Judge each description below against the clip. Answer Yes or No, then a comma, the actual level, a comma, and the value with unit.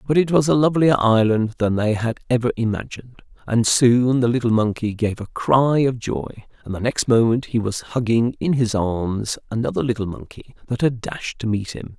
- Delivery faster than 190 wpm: Yes, average, 200 wpm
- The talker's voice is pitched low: Yes, low, 120 Hz